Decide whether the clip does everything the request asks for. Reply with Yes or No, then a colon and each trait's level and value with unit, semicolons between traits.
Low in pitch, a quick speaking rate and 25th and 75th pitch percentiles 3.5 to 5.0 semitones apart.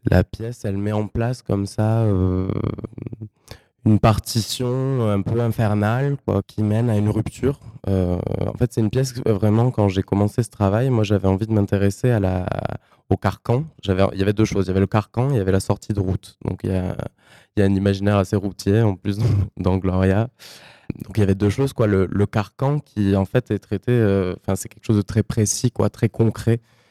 No: low, 105 Hz; fast, 225 wpm; average, 3.0 semitones